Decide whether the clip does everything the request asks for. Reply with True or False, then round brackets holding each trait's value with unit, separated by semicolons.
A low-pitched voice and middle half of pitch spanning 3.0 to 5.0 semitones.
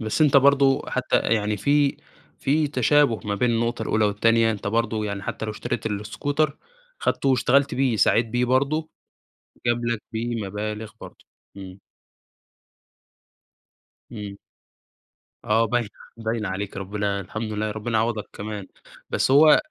True (115 Hz; 3.6 semitones)